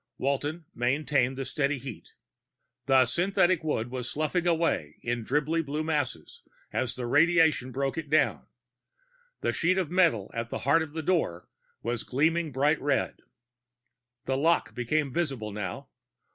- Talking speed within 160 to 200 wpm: No, average, 145 wpm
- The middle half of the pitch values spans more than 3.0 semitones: Yes, average, 4.3 semitones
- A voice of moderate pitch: Yes, medium, 145 Hz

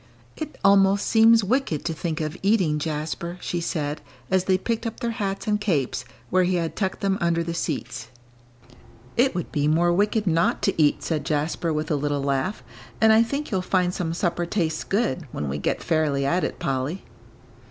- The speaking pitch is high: No, medium, 175 Hz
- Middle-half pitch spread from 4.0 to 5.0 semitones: Yes, average, 4.5 semitones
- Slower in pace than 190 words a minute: No, average, 195 wpm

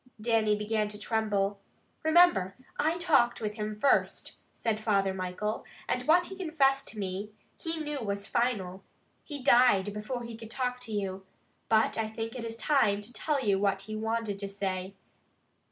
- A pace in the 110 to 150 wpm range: No, average, 170 wpm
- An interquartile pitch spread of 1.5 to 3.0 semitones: No, average, 3.8 semitones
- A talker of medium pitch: No, high, 220 Hz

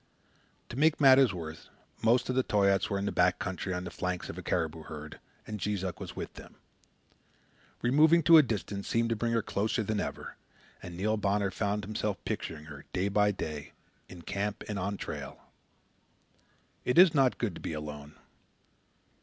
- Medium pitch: No, low, 100 Hz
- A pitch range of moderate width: Yes, average, 4.4 semitones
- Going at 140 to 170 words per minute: No, average, 185 wpm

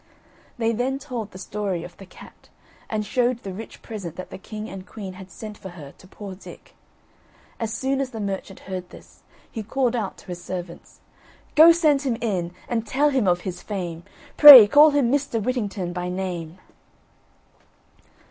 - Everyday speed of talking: Yes, average, 180 wpm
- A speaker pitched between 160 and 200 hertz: No, high, 210 Hz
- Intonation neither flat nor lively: Yes, average, 5.0 semitones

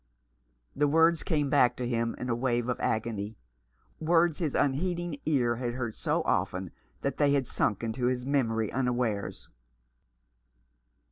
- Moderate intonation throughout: Yes, average, 3.8 semitones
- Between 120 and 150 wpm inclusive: Yes, average, 145 wpm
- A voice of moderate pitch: No, low, 125 Hz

